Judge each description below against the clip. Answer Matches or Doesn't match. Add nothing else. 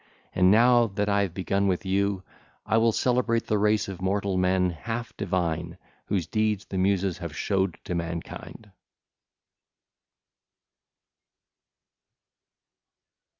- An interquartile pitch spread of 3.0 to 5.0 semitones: Doesn't match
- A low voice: Matches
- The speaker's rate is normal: Doesn't match